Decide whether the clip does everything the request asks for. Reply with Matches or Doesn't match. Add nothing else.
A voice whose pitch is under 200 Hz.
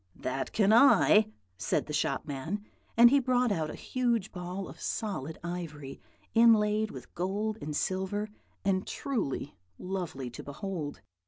Matches